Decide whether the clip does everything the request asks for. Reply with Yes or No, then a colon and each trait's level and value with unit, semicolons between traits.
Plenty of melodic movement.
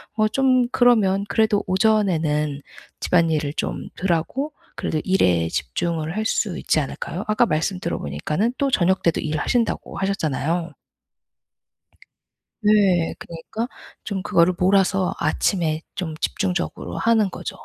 No: average, 4.8 semitones